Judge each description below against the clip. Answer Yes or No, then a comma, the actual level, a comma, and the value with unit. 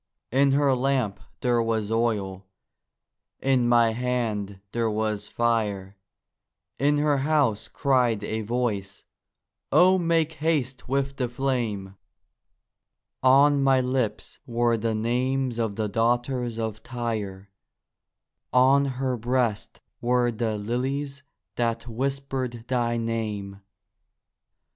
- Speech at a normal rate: No, slow, 110 wpm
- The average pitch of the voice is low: Yes, low, 120 Hz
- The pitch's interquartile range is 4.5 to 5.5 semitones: No, average, 3.2 semitones